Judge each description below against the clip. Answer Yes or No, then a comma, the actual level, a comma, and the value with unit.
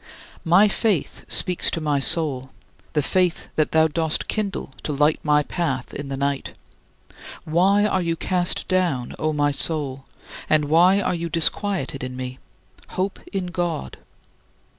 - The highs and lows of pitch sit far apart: No, average, 4.2 semitones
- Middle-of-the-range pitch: Yes, medium, 160 Hz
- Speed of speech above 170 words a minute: No, average, 150 wpm